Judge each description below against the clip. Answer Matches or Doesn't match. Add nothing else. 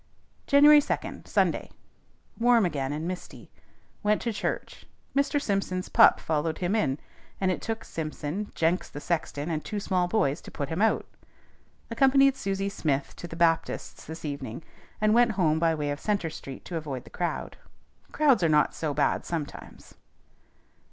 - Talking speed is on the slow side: Doesn't match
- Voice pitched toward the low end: Doesn't match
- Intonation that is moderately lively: Doesn't match